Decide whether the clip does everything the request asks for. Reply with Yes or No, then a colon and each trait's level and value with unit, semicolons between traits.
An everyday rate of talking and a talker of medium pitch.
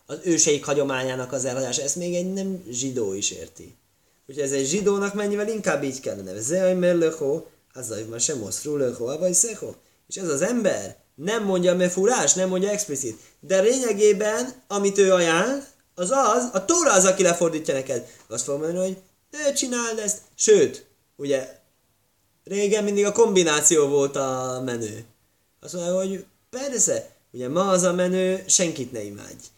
No: fast, 165 wpm; medium, 180 Hz